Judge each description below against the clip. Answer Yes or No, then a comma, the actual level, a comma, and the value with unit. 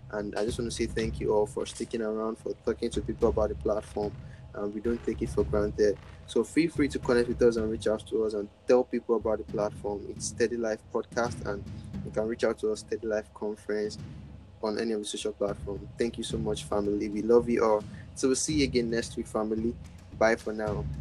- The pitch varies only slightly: Yes, narrow, 2.2 semitones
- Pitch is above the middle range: No, low, 110 Hz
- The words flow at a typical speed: No, fast, 245 wpm